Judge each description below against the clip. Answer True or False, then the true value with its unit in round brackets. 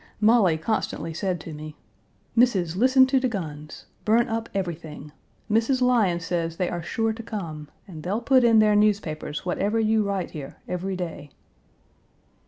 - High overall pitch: True (195 Hz)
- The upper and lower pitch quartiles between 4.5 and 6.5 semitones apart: True (5.3 semitones)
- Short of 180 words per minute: True (160 wpm)